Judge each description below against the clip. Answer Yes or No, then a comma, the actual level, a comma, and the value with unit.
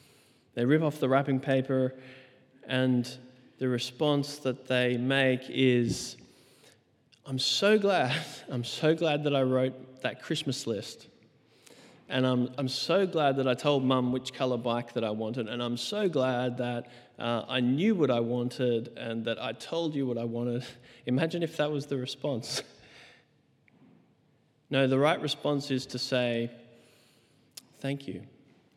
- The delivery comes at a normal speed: Yes, average, 155 wpm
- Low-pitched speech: Yes, low, 130 Hz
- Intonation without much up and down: Yes, narrow, 2.1 semitones